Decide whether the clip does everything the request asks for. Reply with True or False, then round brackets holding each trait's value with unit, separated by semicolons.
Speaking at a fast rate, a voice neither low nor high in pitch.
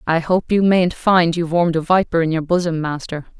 True (230 wpm; 170 Hz)